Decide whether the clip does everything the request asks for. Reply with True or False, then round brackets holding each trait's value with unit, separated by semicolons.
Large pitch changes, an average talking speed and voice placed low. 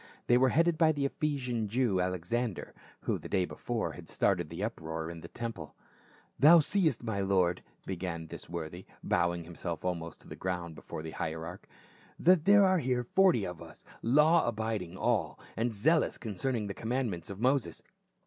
True (7.2 semitones; 170 wpm; 105 Hz)